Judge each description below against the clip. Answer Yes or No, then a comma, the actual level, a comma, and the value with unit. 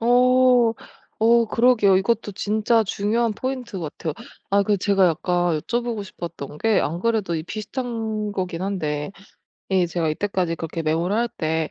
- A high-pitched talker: Yes, high, 200 Hz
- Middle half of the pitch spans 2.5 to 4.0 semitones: No, average, 5.1 semitones